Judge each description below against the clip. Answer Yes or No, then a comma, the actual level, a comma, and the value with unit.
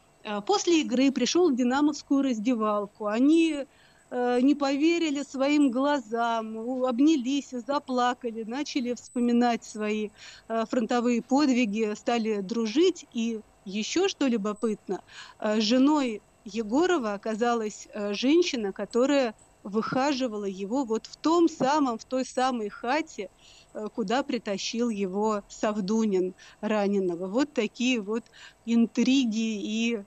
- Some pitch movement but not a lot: Yes, average, 4.1 semitones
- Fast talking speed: No, slow, 110 wpm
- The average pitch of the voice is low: No, high, 240 Hz